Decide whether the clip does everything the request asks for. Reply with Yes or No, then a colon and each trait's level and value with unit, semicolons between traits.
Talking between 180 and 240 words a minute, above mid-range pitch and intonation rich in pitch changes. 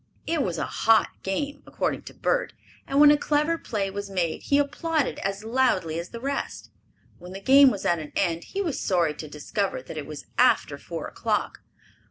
Yes: average, 200 wpm; high, 205 Hz; wide, 8.4 semitones